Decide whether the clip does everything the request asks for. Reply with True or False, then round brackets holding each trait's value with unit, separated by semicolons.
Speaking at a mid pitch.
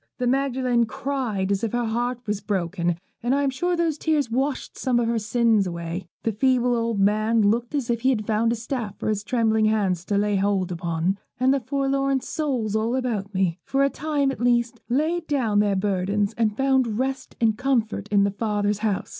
False (230 Hz)